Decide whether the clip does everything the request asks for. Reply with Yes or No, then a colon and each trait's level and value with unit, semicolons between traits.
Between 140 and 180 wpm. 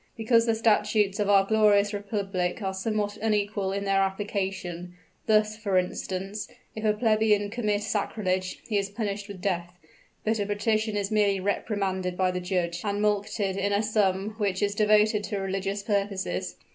Yes: average, 165 wpm